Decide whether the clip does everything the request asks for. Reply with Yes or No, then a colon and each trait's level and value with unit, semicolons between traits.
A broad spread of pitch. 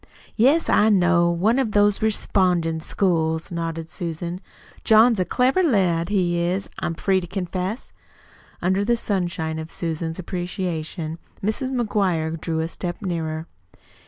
No: average, 3.8 semitones